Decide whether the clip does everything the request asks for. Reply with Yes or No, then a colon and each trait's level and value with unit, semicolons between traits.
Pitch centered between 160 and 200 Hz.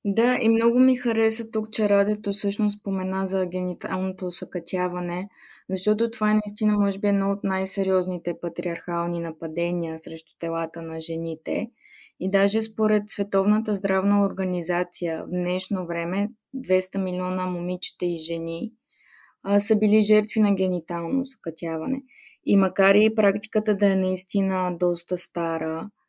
Yes: high, 190 Hz